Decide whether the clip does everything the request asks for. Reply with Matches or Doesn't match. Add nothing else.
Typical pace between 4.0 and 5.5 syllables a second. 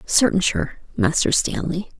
Matches